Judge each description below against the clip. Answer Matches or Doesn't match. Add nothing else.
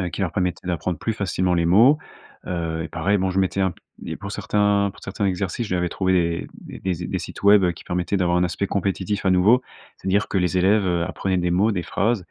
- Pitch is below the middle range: Matches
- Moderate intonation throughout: Doesn't match